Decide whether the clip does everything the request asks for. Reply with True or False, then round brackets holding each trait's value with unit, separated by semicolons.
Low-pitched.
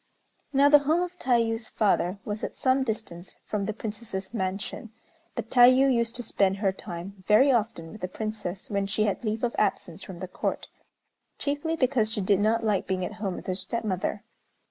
False (215 Hz)